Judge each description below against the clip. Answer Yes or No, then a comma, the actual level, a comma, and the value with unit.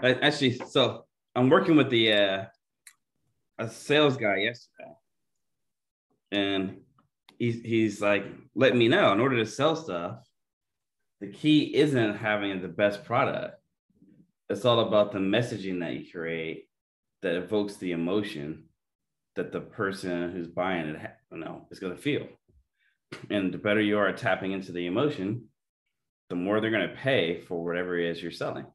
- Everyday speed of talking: Yes, average, 160 wpm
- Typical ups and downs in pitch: Yes, average, 4.5 semitones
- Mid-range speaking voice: No, low, 100 Hz